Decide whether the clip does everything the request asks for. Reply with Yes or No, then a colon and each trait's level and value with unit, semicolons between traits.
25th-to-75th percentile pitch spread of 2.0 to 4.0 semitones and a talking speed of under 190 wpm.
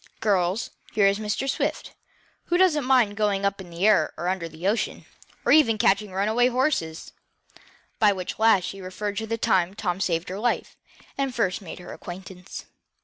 Yes: average, 3.6 semitones; average, 180 wpm